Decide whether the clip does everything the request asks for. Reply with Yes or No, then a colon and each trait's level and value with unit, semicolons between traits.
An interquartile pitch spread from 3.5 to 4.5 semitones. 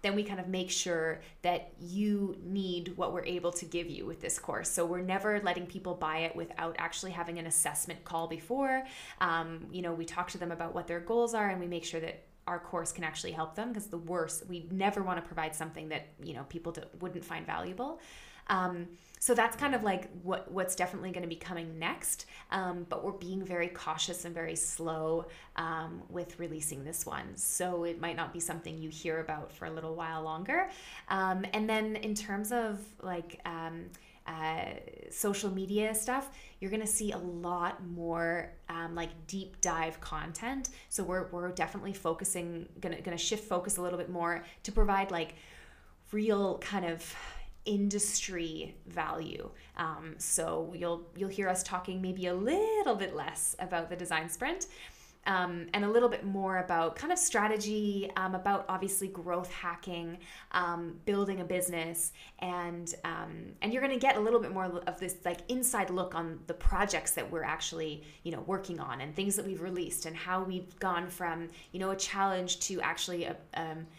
No: narrow, 2.6 semitones